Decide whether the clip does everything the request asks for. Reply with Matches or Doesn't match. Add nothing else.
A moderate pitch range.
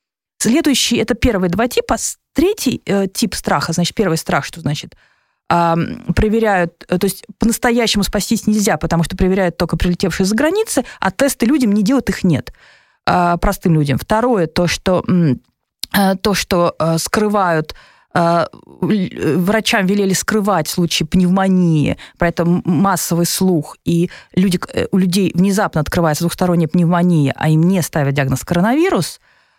Matches